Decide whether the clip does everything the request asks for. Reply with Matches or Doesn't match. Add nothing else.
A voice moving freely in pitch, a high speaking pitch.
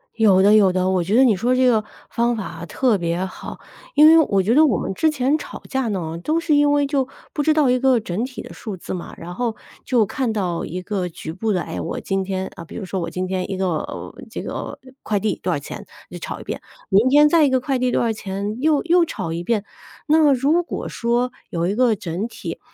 Matches